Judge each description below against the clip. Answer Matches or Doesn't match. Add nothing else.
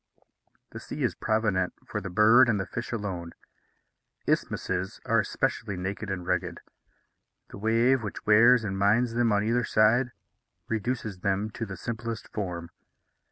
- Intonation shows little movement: Doesn't match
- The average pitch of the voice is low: Matches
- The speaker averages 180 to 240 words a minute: Doesn't match